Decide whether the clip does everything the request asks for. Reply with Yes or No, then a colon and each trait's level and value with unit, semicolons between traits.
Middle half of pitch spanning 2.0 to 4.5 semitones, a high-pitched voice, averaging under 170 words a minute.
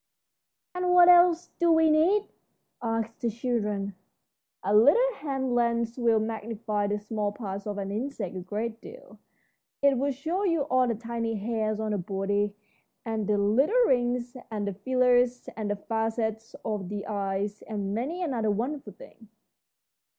Yes: average, 4.1 semitones; high, 225 Hz; average, 160 wpm